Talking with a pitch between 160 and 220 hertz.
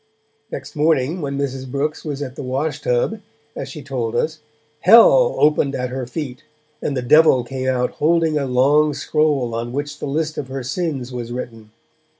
No: medium, 140 Hz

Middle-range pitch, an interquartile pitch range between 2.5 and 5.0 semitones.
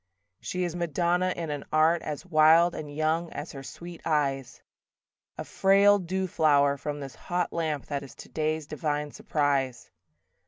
Yes: medium, 155 Hz; average, 2.9 semitones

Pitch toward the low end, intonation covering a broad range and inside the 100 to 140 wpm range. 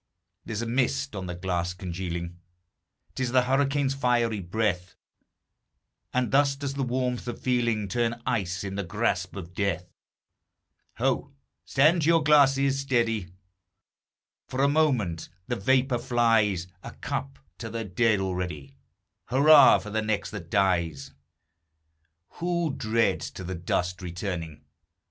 Yes: low, 115 Hz; wide, 6.5 semitones; slow, 135 wpm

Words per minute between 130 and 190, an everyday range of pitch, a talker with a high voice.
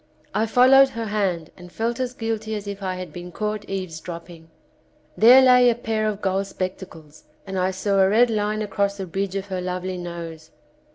No: fast, 205 wpm; average, 3.2 semitones; high, 195 Hz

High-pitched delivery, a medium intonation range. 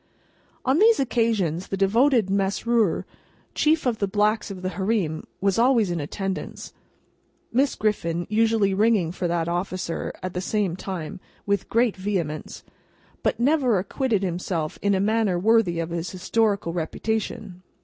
Yes: high, 200 Hz; average, 4.0 semitones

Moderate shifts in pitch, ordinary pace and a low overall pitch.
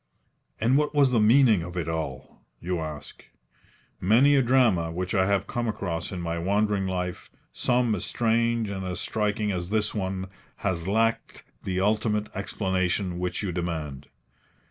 Yes: average, 3.9 semitones; average, 160 wpm; low, 100 Hz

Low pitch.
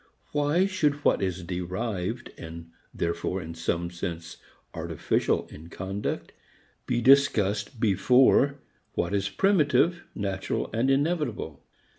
Yes: low, 100 Hz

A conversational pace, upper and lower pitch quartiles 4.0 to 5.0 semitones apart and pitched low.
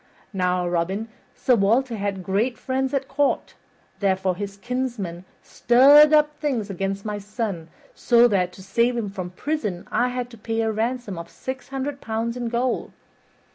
No: average, 165 wpm; average, 4.6 semitones; high, 225 Hz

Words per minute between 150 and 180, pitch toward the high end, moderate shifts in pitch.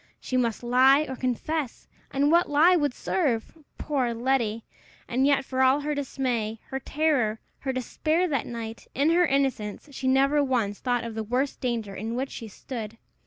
Yes: average, 175 wpm; very high, 260 Hz; average, 3.6 semitones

